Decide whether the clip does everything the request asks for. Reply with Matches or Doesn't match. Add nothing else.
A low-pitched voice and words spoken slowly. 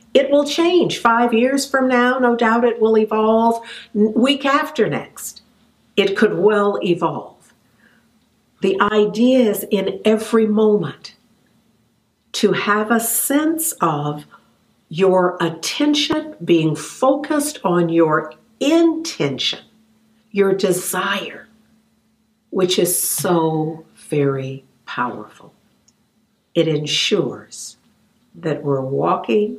Doesn't match